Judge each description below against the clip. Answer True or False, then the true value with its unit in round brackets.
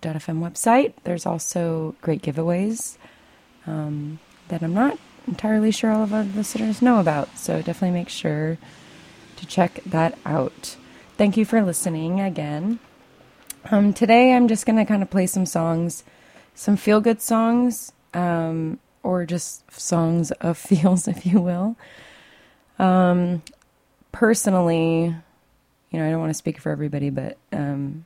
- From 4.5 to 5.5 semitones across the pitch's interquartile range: True (4.8 semitones)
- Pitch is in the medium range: True (180 Hz)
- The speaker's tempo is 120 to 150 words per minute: True (145 wpm)